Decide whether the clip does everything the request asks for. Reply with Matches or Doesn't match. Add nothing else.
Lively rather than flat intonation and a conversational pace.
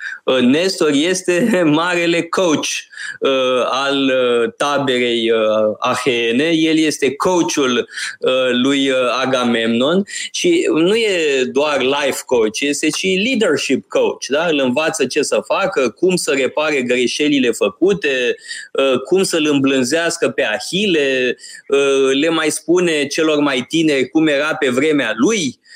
Matches